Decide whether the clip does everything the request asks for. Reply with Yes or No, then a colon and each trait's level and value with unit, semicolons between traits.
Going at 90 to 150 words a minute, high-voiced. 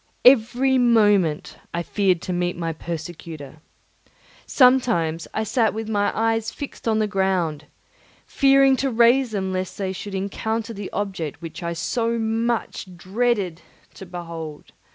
Yes: average, 140 wpm; high, 200 Hz